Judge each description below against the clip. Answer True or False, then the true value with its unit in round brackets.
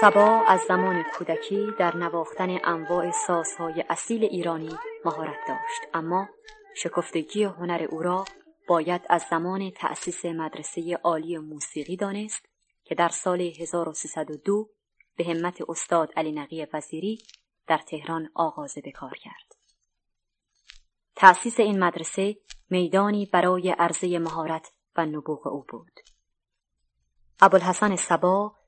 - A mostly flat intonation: False (3.5 semitones)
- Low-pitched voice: False (175 Hz)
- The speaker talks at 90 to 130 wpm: True (110 wpm)